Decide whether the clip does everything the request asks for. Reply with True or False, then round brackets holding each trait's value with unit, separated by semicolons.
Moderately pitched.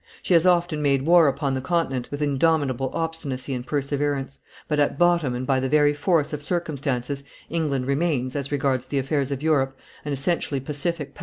True (145 Hz)